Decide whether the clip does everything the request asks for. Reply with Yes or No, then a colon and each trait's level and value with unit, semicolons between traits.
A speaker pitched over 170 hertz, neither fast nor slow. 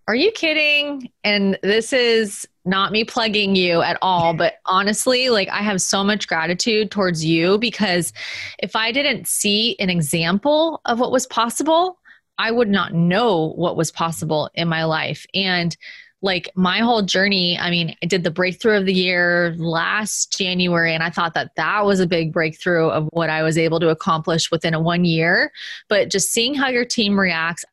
Yes: high, 190 Hz; average, 185 wpm